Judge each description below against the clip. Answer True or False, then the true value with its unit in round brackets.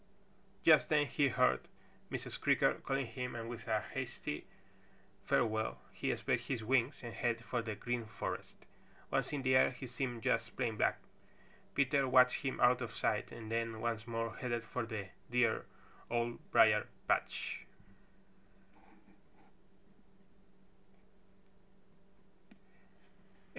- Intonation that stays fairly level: True (1.9 semitones)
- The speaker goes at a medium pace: False (125 wpm)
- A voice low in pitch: True (120 Hz)